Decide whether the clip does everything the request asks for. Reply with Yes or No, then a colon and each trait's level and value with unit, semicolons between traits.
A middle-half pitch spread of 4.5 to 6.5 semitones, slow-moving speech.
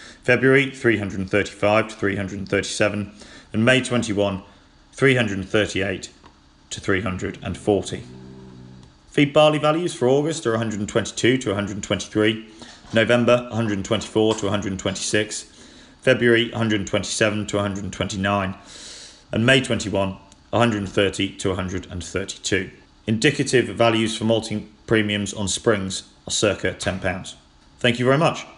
No: average, 3.0 semitones; slow, 100 wpm